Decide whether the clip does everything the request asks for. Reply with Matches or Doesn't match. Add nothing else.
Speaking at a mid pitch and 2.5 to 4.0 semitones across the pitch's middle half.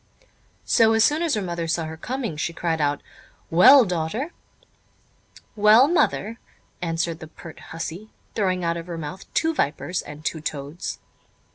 Doesn't match